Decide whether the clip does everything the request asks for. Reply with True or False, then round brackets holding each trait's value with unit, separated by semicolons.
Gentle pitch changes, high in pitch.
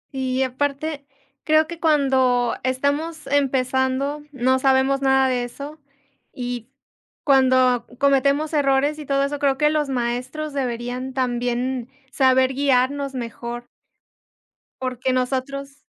True (1.8 semitones; 265 Hz)